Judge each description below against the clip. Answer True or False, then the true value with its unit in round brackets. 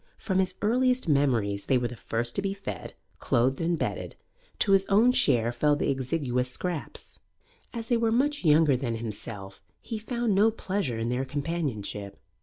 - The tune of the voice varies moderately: False (8.8 semitones)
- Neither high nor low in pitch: True (150 Hz)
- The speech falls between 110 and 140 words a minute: False (175 wpm)